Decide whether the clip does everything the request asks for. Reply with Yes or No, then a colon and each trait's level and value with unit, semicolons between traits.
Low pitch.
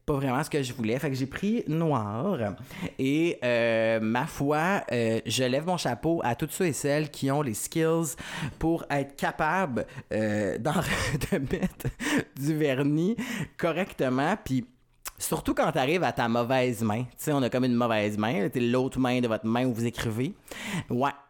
Yes: low, 130 Hz